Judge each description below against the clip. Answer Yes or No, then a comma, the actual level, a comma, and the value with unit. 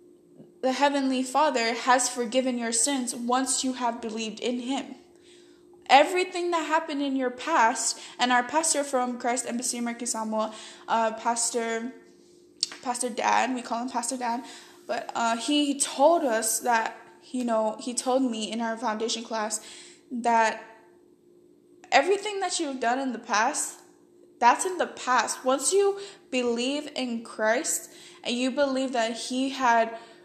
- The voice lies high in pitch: Yes, very high, 255 Hz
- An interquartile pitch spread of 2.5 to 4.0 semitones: No, wide, 5.4 semitones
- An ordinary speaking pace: Yes, average, 145 wpm